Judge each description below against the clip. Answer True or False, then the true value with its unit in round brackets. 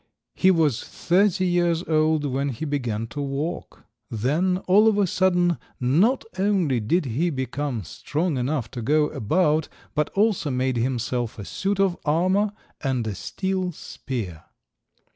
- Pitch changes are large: True (6.1 semitones)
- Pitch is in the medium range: True (155 Hz)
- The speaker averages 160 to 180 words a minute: False (145 wpm)